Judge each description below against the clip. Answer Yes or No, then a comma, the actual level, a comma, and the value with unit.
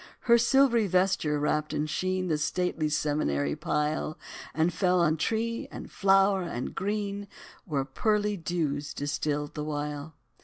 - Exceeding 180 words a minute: No, average, 140 wpm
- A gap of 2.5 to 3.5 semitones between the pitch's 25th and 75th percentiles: No, average, 4.8 semitones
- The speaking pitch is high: No, medium, 160 Hz